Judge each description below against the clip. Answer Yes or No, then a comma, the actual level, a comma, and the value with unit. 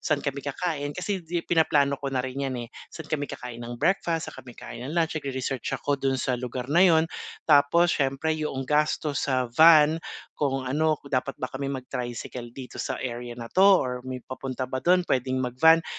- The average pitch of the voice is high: No, medium, 140 Hz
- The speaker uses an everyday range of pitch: Yes, average, 3.7 semitones